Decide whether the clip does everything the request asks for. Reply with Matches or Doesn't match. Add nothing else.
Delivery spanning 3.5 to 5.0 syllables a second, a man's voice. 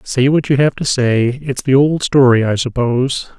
Matches